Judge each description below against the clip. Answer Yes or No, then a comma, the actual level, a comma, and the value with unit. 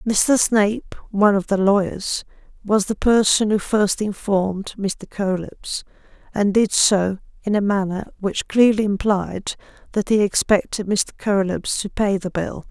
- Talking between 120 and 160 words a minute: Yes, average, 150 wpm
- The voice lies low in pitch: No, high, 200 Hz